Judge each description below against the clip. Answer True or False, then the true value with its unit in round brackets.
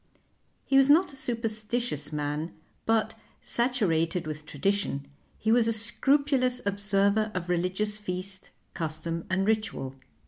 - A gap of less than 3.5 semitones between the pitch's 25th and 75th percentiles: False (5.3 semitones)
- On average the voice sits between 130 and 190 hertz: False (205 Hz)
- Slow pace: True (125 wpm)